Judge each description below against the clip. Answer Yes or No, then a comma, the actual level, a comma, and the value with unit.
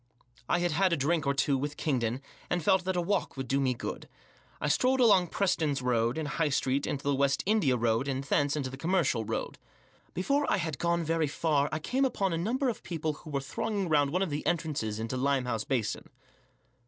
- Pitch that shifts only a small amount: No, average, 4.6 semitones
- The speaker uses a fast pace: Yes, fast, 215 wpm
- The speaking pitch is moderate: Yes, medium, 150 Hz